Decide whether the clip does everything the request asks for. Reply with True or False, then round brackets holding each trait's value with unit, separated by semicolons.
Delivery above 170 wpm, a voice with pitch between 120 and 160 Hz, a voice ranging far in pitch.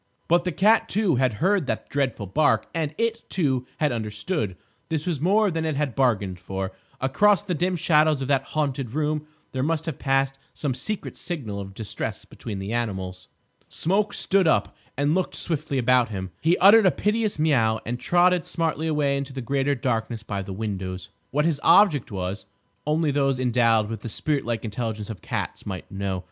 True (185 wpm; 135 Hz; 6.5 semitones)